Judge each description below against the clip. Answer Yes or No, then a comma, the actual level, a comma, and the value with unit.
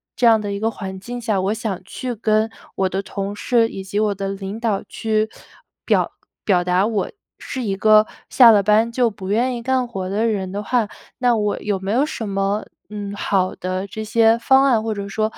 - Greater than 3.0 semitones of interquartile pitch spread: No, average, 2.7 semitones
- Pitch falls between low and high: No, high, 215 Hz